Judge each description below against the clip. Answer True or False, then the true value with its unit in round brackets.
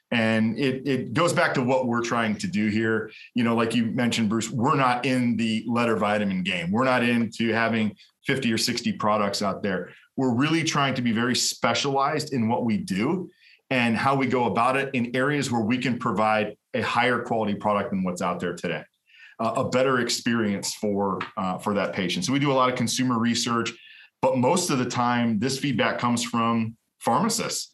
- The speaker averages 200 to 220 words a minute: True (205 wpm)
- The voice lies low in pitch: True (120 Hz)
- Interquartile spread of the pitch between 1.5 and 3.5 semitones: True (2.8 semitones)